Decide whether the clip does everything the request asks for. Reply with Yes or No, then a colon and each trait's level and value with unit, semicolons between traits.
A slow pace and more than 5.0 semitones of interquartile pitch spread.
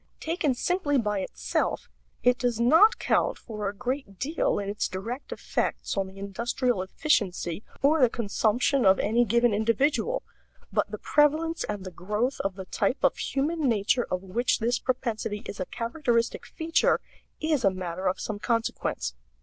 No: average, 165 wpm; wide, 5.4 semitones